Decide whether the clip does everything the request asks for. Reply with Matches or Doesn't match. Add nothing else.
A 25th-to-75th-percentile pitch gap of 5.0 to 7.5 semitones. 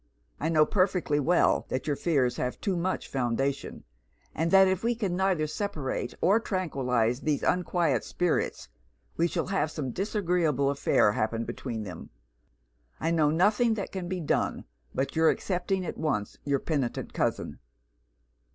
Matches